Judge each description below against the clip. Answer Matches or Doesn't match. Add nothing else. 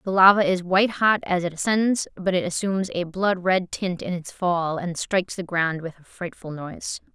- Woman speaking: Matches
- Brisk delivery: Matches